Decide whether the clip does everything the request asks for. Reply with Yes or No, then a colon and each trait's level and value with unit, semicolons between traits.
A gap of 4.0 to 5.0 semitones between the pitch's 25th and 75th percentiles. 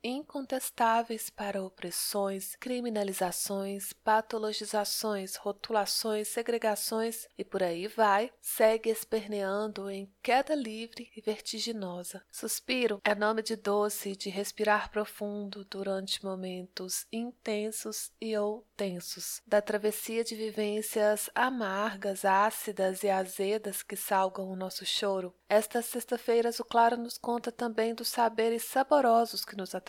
No: narrow, 2.5 semitones